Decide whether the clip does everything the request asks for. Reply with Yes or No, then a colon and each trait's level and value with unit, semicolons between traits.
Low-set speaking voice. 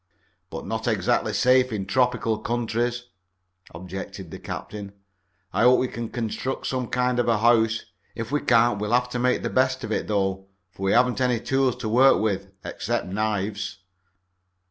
Yes: low, 115 Hz